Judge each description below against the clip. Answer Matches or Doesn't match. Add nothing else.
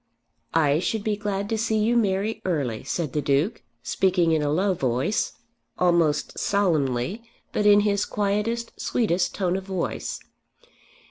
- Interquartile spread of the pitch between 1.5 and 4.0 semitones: Doesn't match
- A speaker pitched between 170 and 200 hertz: Matches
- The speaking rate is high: Doesn't match